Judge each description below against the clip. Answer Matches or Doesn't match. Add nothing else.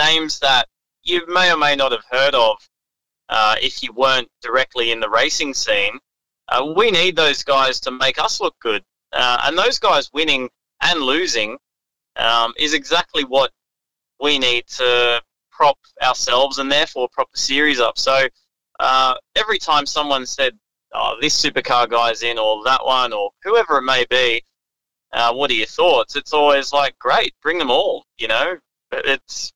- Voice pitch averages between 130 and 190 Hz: Matches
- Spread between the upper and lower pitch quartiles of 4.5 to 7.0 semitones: Doesn't match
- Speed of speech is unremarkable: Matches